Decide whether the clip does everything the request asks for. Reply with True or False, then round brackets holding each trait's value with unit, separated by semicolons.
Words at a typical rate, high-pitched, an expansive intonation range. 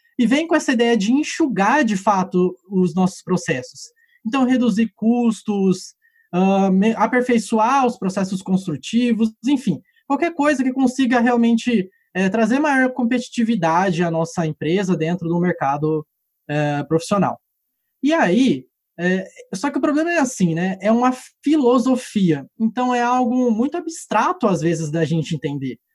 True (140 wpm; 225 Hz; 6.2 semitones)